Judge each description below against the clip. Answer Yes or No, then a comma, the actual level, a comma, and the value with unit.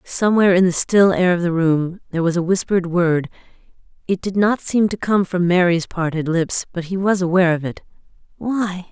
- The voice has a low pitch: No, medium, 180 Hz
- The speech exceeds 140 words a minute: Yes, average, 200 wpm